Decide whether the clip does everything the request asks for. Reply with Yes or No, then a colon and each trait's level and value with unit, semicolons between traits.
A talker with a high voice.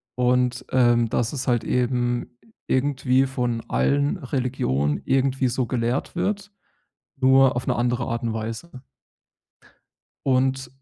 No: low, 125 Hz